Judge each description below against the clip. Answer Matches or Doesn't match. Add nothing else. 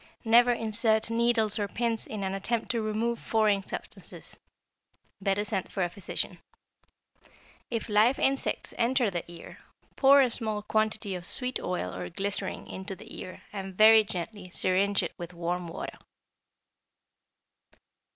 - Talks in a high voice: Matches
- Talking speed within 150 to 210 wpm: Doesn't match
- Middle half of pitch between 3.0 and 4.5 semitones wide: Matches